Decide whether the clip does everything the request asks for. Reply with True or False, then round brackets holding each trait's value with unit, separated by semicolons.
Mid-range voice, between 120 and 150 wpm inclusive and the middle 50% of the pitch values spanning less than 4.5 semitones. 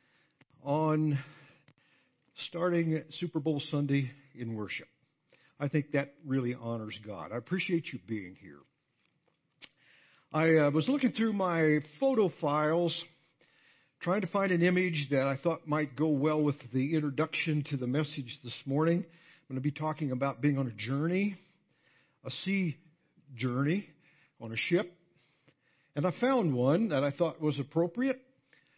True (150 Hz; 145 wpm; 3.5 semitones)